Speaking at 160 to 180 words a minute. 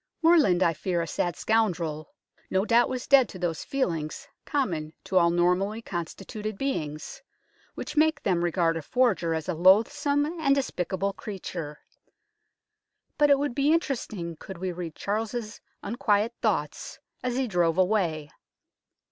No: average, 145 wpm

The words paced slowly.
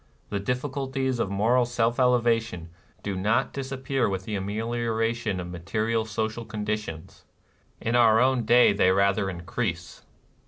No: average, 155 wpm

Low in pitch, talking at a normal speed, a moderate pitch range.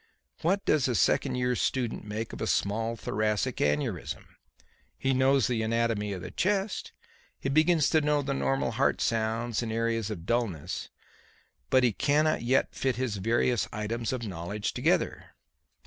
Yes: low, 115 Hz; average, 160 wpm; average, 3.8 semitones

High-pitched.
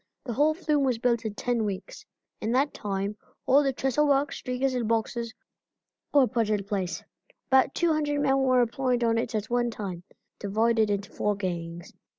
Yes: high, 235 Hz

